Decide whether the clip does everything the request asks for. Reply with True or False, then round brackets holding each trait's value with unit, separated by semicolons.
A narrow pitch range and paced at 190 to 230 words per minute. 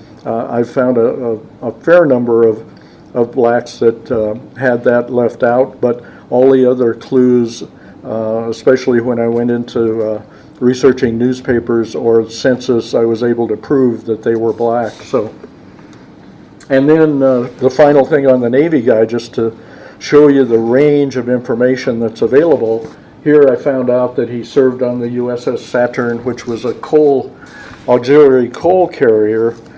False (2.1 semitones; 165 wpm)